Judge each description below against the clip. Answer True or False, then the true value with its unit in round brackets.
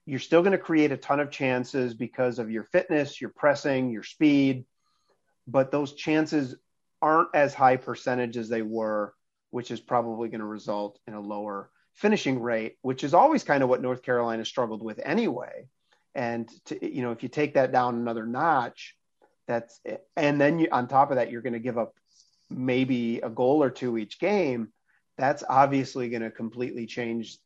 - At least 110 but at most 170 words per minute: False (190 wpm)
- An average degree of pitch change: True (3.3 semitones)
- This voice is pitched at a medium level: False (125 Hz)